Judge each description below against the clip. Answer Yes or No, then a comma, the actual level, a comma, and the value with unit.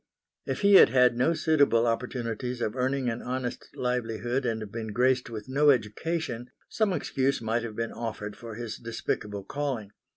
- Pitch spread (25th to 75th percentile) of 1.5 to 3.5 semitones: Yes, narrow, 2.6 semitones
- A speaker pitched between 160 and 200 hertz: No, low, 120 Hz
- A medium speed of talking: Yes, average, 165 wpm